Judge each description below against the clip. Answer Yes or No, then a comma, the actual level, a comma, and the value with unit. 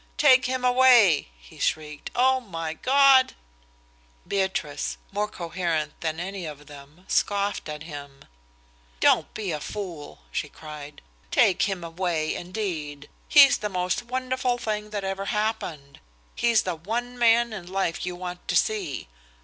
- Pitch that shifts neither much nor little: No, wide, 6.1 semitones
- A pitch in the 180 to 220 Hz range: Yes, medium, 185 Hz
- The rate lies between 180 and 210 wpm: No, average, 140 wpm